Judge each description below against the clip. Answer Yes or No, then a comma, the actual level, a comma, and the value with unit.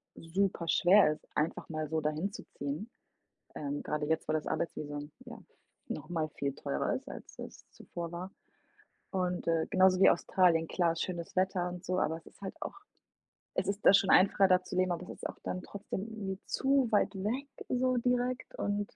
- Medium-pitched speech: Yes, medium, 180 Hz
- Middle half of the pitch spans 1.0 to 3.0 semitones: No, average, 3.7 semitones